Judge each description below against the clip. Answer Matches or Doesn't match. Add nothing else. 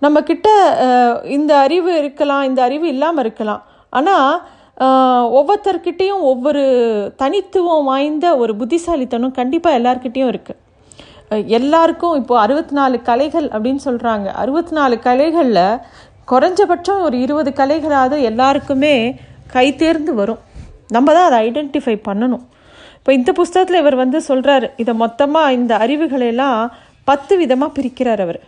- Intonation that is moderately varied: Matches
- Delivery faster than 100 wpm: Matches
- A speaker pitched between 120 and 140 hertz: Doesn't match